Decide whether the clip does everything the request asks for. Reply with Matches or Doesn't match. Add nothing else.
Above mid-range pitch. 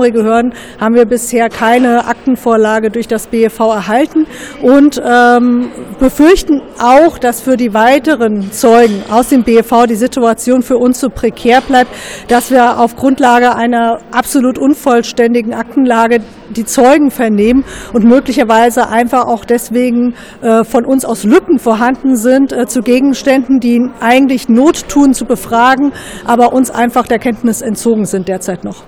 Matches